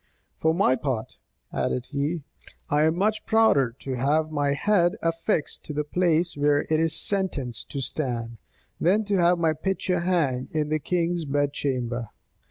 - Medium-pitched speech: Yes, medium, 155 Hz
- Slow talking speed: No, average, 165 wpm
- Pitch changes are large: No, average, 3.9 semitones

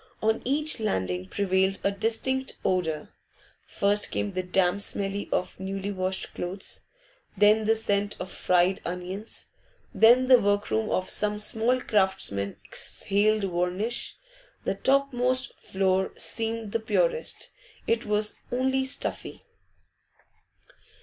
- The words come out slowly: Yes, slow, 115 wpm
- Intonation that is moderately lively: Yes, average, 3.3 semitones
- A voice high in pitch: Yes, high, 205 Hz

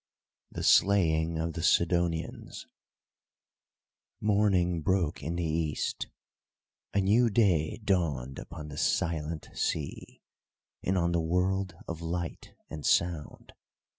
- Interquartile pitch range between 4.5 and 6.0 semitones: No, narrow, 2.6 semitones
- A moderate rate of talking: No, slow, 110 wpm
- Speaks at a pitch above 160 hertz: No, very low, 85 Hz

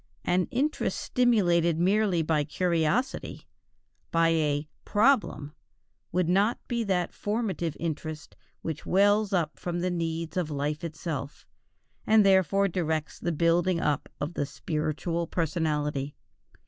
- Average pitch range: Yes, average, 3.7 semitones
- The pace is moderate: No, slow, 120 wpm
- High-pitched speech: No, medium, 170 Hz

